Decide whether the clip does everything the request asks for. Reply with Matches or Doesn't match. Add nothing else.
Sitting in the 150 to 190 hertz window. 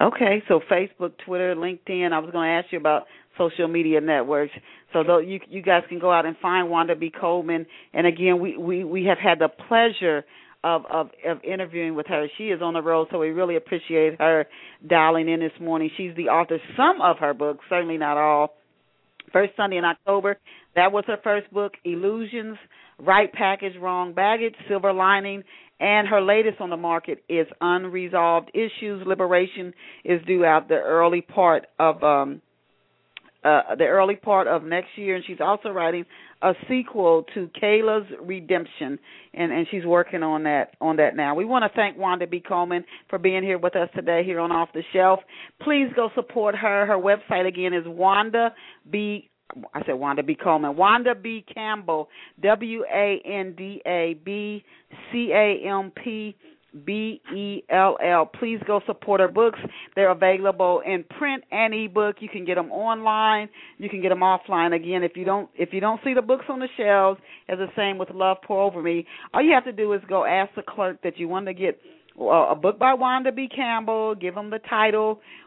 Matches